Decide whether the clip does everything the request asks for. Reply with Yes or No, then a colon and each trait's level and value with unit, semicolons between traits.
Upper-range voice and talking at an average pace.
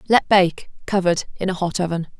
No: medium, 180 Hz; average, 190 wpm